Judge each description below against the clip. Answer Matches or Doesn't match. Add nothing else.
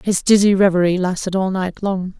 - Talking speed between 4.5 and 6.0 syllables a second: Matches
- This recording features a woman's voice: Matches